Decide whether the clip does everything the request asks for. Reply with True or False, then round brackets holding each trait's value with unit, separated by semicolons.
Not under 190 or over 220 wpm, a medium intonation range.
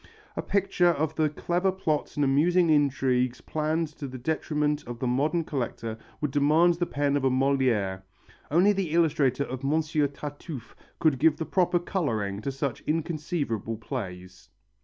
False (160 wpm; 3.9 semitones)